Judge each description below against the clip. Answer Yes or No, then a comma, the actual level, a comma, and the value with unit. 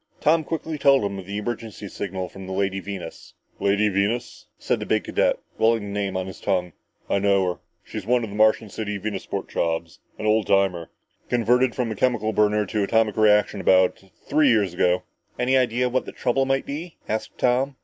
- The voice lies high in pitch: No, low, 105 Hz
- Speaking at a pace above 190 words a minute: Yes, average, 200 wpm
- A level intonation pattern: No, average, 4.0 semitones